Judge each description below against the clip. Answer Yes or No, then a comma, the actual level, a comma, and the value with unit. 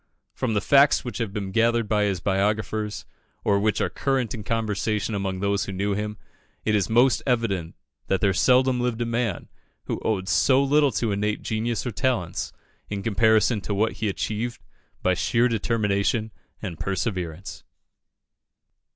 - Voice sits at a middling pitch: No, low, 105 Hz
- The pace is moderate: Yes, average, 160 wpm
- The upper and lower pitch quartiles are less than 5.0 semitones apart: Yes, average, 2.9 semitones